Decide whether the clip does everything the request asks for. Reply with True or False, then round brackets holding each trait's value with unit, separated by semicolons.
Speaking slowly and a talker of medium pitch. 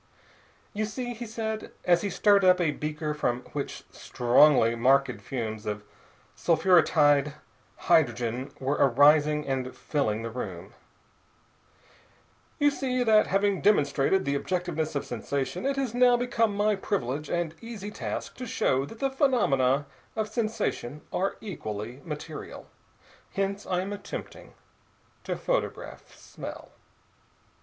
True (130 wpm; 160 Hz)